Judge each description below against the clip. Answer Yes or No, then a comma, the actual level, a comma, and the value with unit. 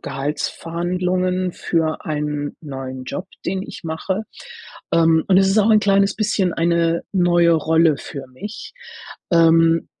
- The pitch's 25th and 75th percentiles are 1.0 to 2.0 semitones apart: No, average, 2.7 semitones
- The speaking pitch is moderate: Yes, medium, 170 Hz